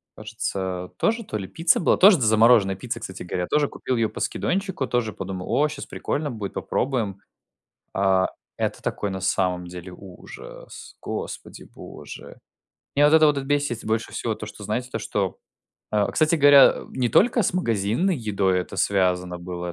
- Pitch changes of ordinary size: No, wide, 7.2 semitones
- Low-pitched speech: Yes, low, 110 Hz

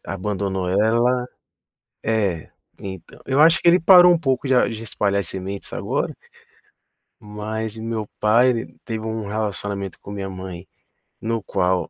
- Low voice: Yes, low, 105 Hz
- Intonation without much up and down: No, average, 3.1 semitones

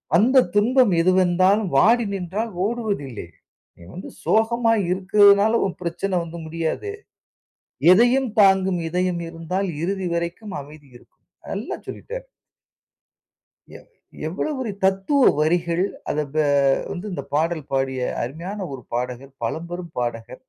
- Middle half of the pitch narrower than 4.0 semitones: No, average, 4.5 semitones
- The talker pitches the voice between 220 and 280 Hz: No, medium, 185 Hz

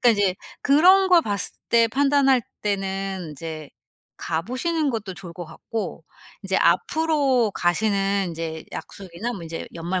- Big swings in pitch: Yes, wide, 7.2 semitones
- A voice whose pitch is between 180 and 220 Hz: Yes, high, 200 Hz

